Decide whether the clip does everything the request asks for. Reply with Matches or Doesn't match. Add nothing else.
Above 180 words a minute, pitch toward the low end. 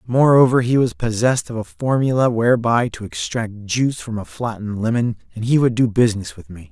Matches